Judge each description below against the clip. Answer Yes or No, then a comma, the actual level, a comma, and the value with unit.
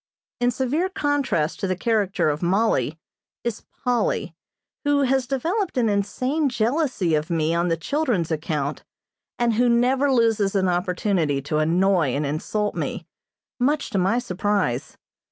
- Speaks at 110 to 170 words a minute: Yes, average, 145 wpm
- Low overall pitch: No, high, 210 Hz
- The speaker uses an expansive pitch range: Yes, wide, 7.0 semitones